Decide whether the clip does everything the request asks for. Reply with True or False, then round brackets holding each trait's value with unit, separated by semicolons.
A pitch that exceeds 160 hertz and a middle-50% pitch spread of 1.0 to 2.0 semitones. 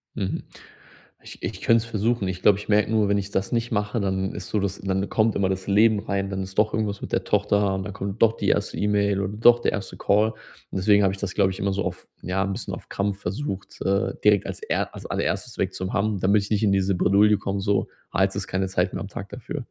False (100 Hz; 1.5 semitones)